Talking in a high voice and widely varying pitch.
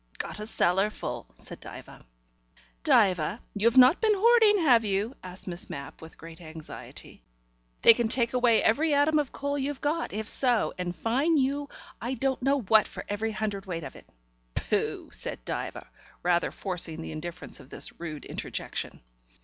Yes: high, 220 Hz; wide, 7.4 semitones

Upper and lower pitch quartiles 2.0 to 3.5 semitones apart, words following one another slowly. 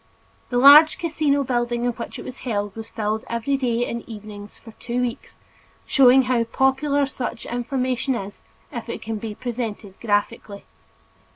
No: average, 3.0 semitones; average, 160 wpm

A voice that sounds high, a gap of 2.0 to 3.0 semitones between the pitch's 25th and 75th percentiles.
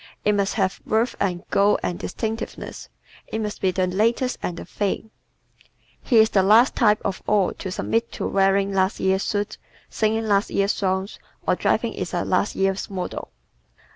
Yes: high, 200 Hz; narrow, 2.4 semitones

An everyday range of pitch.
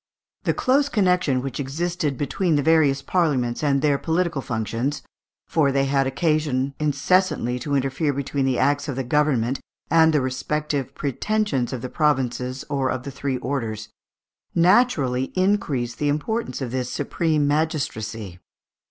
Yes: average, 3.3 semitones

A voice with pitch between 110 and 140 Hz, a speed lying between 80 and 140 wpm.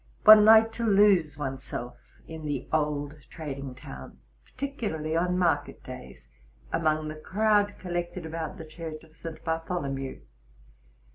No: medium, 160 Hz; slow, 135 wpm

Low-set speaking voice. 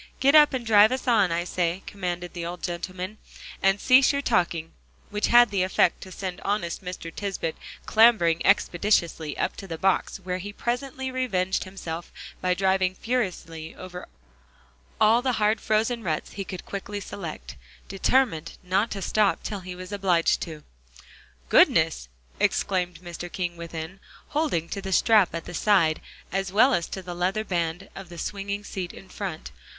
No: high, 190 Hz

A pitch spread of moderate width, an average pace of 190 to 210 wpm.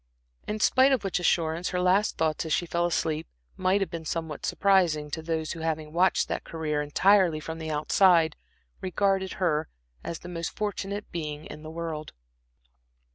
No: average, 3.1 semitones; average, 175 wpm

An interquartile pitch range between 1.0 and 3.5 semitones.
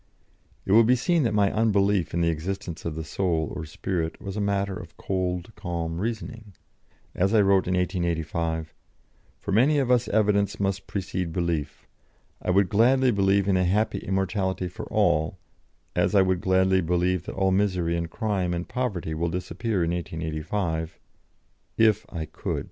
Yes: average, 3.2 semitones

